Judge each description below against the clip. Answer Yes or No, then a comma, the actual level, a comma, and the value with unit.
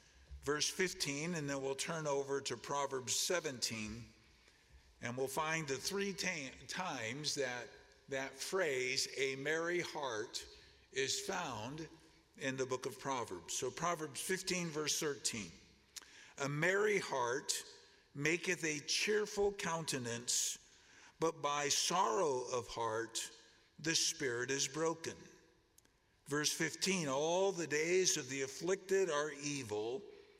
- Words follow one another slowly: Yes, slow, 120 wpm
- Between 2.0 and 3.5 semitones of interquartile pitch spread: No, wide, 5.5 semitones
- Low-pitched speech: No, medium, 155 Hz